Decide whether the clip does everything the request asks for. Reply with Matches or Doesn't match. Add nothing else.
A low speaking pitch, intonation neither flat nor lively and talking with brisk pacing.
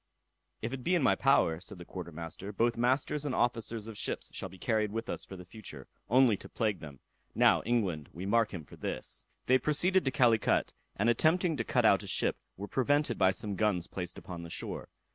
Doesn't match